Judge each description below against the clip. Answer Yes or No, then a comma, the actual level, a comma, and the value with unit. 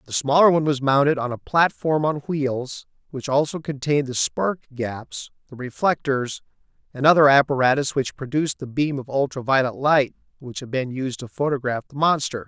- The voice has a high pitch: No, low, 135 Hz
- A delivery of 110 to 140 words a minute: No, average, 180 wpm